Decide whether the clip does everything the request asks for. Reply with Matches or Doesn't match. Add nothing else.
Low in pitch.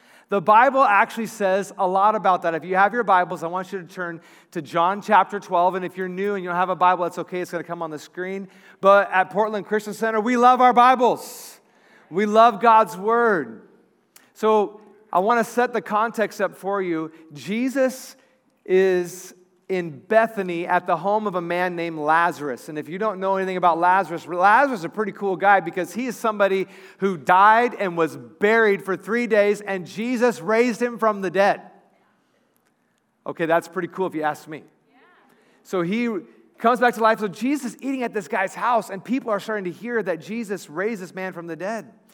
Doesn't match